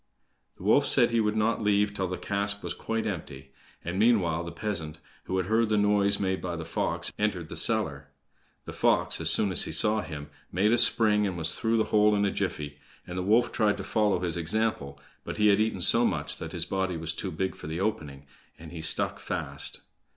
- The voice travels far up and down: No, average, 4.0 semitones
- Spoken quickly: Yes, fast, 225 wpm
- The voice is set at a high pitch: No, low, 100 Hz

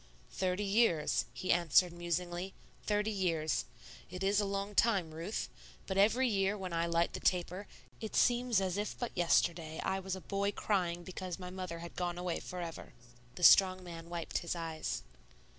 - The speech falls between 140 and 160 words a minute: No, average, 175 wpm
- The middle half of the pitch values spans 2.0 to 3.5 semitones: Yes, narrow, 2.6 semitones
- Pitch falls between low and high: Yes, medium, 180 Hz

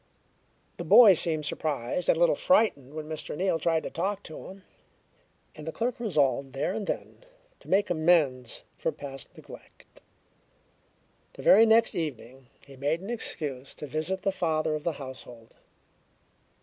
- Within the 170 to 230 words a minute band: No, average, 160 wpm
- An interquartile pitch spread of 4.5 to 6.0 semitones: Yes, average, 5.3 semitones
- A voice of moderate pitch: Yes, medium, 155 Hz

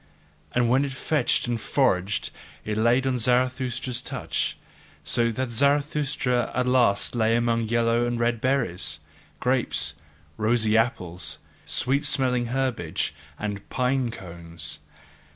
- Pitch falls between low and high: No, low, 120 Hz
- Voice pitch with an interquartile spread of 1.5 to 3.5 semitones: Yes, average, 2.7 semitones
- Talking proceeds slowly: Yes, slow, 120 wpm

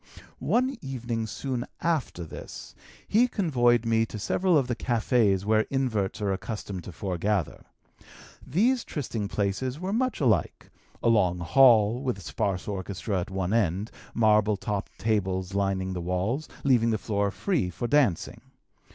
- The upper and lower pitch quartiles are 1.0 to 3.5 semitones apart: No, average, 5.1 semitones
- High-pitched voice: No, low, 110 Hz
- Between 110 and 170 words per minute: Yes, average, 145 wpm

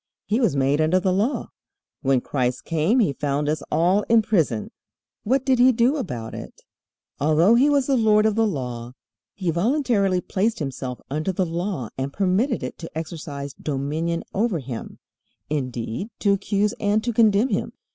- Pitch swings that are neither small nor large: No, wide, 7.3 semitones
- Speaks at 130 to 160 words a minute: No, average, 170 wpm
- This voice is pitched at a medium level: Yes, medium, 180 Hz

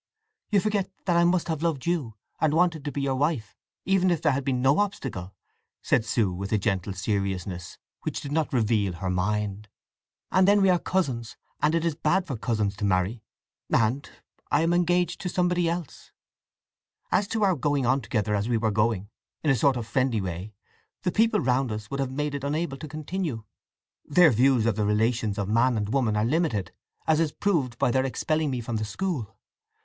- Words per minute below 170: No, average, 200 wpm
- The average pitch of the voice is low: Yes, low, 130 Hz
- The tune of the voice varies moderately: No, wide, 7.4 semitones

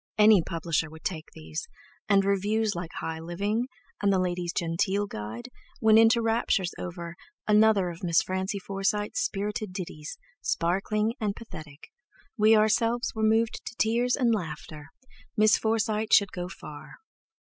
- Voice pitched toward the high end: Yes, high, 200 Hz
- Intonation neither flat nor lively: Yes, average, 4.1 semitones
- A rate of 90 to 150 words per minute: Yes, average, 145 wpm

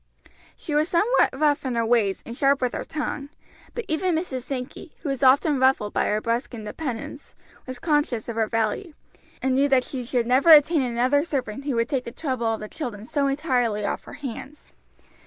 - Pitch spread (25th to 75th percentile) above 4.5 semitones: No, average, 3.9 semitones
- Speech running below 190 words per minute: No, average, 200 wpm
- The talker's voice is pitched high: Yes, very high, 260 Hz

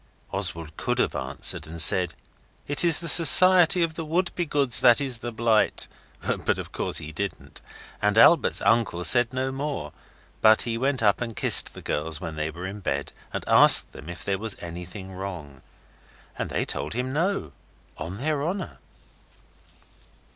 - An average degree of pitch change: No, wide, 8.6 semitones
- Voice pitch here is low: Yes, low, 115 Hz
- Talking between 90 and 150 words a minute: No, average, 170 wpm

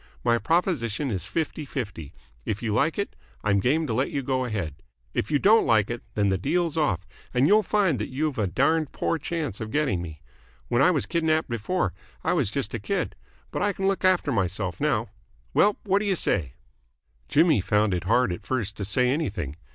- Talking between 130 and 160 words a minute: No, fast, 205 wpm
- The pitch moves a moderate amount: No, wide, 8.0 semitones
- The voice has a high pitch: No, low, 130 Hz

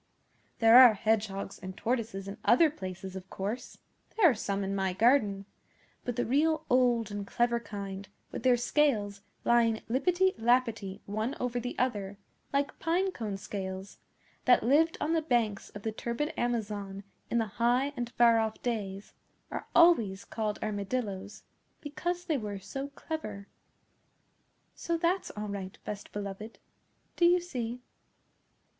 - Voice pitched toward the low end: No, high, 230 Hz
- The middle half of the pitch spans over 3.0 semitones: Yes, average, 4.4 semitones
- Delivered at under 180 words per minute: Yes, average, 150 wpm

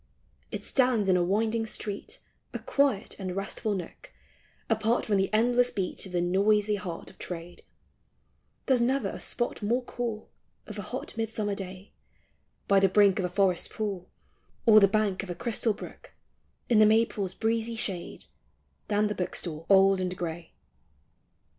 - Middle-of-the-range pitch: No, high, 205 Hz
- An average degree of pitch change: Yes, average, 3.2 semitones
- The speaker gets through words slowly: No, average, 165 wpm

